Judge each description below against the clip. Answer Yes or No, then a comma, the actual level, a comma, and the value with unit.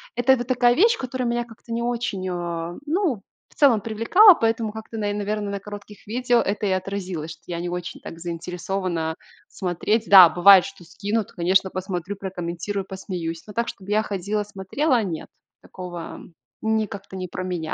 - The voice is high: Yes, high, 200 Hz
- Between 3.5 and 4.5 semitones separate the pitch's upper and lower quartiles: Yes, average, 4.0 semitones